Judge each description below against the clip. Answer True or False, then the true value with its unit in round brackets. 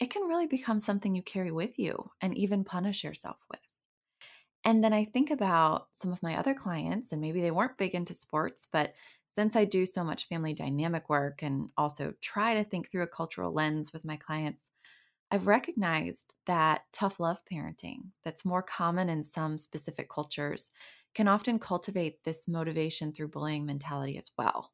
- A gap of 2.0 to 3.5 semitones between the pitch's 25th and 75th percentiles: False (4.8 semitones)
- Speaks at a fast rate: False (180 wpm)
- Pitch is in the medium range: True (175 Hz)